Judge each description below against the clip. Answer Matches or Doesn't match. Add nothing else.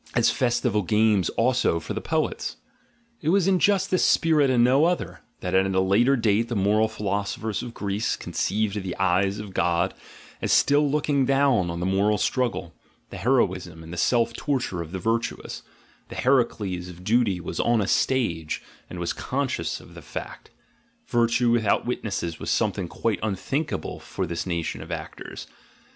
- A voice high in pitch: Doesn't match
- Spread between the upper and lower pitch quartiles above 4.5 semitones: Matches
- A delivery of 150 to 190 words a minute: Matches